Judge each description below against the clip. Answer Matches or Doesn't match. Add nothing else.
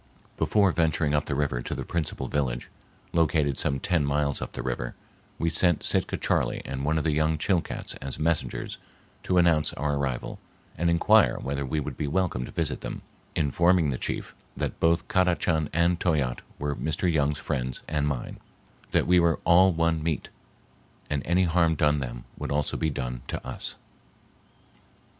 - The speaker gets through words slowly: Doesn't match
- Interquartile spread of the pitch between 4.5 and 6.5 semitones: Doesn't match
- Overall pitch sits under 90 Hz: Matches